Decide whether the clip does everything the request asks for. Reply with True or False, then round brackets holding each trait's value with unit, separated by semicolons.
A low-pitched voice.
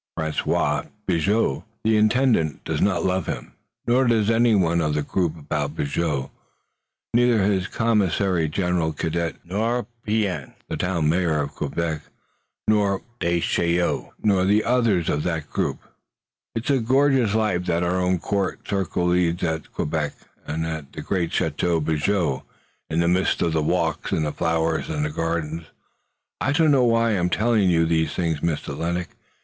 True (90 Hz)